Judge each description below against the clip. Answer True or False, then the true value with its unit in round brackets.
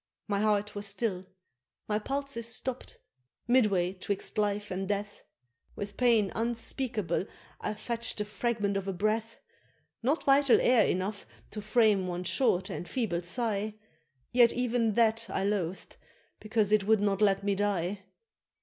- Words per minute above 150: False (145 wpm)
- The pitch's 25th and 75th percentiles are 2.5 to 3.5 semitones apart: True (2.8 semitones)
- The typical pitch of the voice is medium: False (210 Hz)